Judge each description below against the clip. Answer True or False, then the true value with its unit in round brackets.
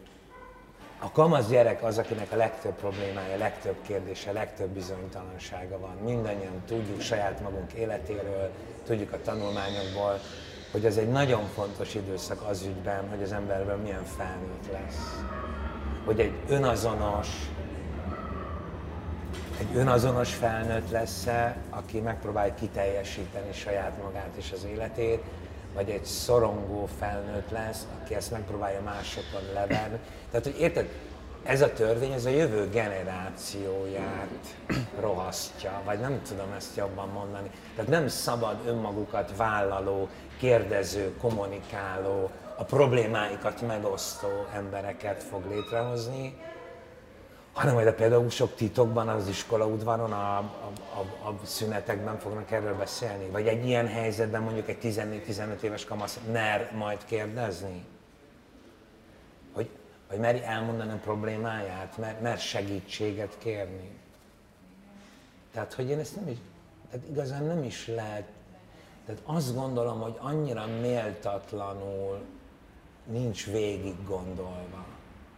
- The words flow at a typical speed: True (120 wpm)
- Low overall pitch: True (105 Hz)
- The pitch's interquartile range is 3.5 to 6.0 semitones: False (2.7 semitones)